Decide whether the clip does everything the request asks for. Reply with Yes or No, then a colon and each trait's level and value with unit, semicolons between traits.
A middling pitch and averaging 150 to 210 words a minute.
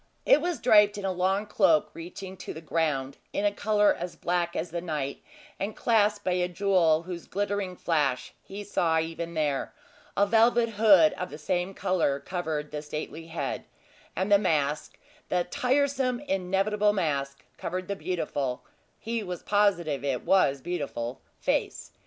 Yes: medium, 180 Hz; average, 160 wpm